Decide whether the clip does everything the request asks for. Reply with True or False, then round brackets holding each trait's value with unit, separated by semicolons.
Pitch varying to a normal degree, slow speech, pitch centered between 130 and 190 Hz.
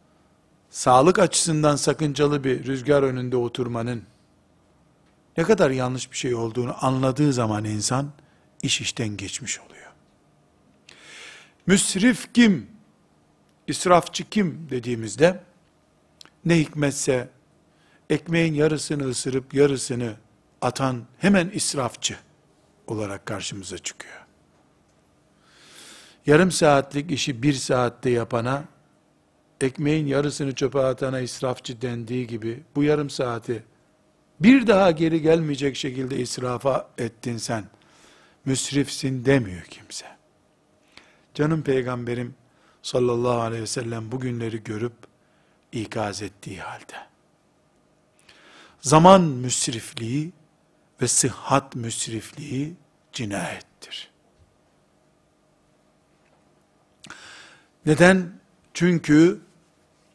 True (4.2 semitones; 85 wpm; 135 Hz)